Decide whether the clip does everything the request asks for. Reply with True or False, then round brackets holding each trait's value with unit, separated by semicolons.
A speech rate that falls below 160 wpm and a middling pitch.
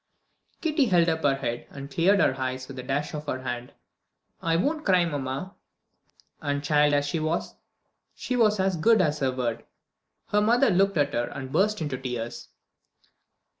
False (175 wpm; 150 Hz)